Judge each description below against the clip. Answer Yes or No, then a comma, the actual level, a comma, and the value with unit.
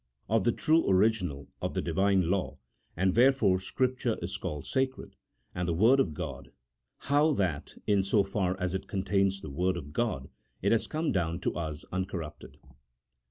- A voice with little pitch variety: No, average, 4.3 semitones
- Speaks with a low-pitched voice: Yes, very low, 95 Hz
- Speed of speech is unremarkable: Yes, average, 175 wpm